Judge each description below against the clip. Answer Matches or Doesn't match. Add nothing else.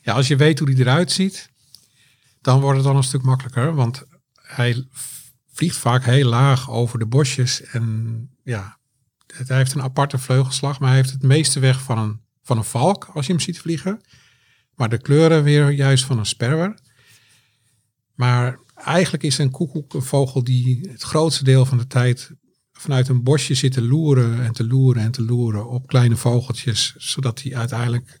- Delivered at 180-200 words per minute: Matches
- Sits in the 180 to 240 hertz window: Doesn't match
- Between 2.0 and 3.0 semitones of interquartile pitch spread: Matches